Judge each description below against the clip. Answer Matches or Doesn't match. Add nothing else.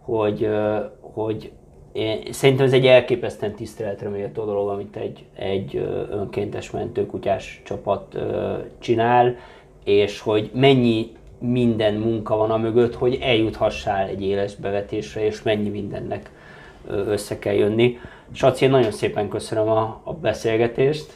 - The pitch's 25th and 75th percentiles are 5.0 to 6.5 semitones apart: Doesn't match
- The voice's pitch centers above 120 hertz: Doesn't match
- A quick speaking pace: Doesn't match